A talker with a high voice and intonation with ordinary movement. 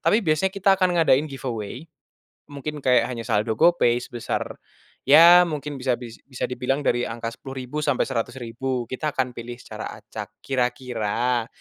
No: low, 130 Hz; average, 3.7 semitones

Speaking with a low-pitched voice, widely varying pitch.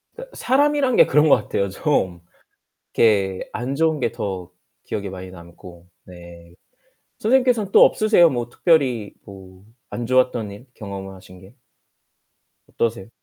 Yes: low, 110 Hz; wide, 8.7 semitones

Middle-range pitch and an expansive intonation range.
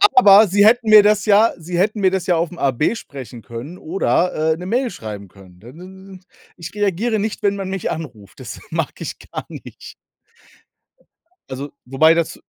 Yes: medium, 180 Hz; wide, 6.4 semitones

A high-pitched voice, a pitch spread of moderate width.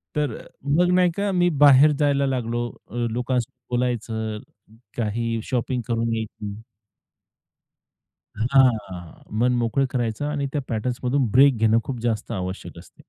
No: low, 120 Hz; average, 3.6 semitones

